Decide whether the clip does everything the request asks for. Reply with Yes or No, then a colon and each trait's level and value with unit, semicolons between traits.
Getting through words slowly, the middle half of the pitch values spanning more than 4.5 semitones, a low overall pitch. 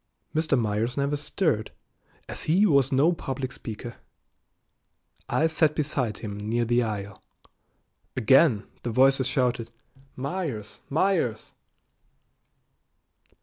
Yes: slow, 105 wpm; average, 5.1 semitones; low, 130 Hz